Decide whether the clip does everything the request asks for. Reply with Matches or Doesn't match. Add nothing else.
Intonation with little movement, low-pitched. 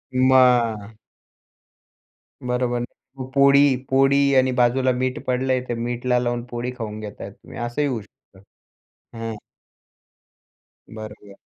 Matches